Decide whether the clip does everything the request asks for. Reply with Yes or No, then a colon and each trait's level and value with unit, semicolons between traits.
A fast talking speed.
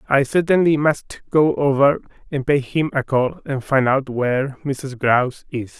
No: average, 175 wpm